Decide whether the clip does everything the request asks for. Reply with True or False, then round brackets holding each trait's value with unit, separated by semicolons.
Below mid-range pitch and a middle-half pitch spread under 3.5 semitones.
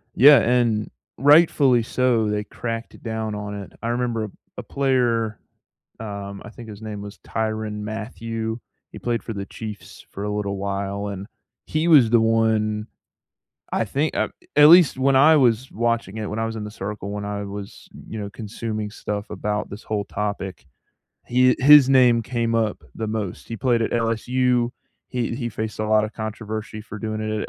True (110 Hz; 2.4 semitones)